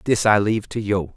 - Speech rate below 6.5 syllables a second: Yes, 5.9 syllables/s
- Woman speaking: No, male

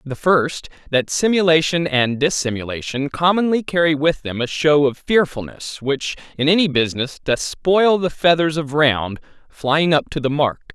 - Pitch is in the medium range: Yes, medium, 150 Hz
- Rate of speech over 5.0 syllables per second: No, 4.6 syllables/s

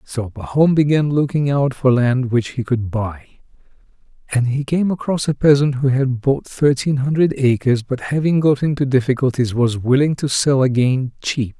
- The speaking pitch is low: Yes, low, 130 Hz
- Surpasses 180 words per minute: No, average, 175 wpm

